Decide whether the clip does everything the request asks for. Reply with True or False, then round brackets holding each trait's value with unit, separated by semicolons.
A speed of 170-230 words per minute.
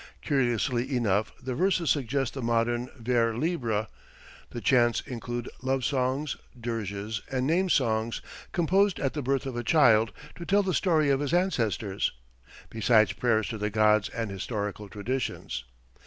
False (150 wpm)